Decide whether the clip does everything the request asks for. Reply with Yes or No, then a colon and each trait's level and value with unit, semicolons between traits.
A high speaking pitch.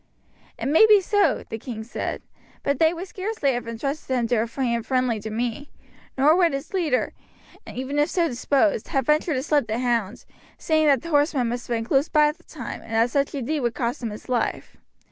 Yes: very high, 270 Hz